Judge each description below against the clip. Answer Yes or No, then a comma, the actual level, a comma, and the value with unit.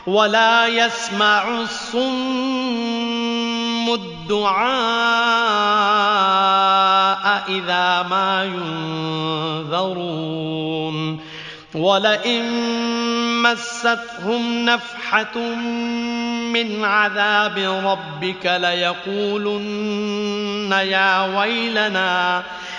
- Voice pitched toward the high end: Yes, high, 210 Hz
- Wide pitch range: No, average, 3.8 semitones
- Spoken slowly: Yes, slow, 45 wpm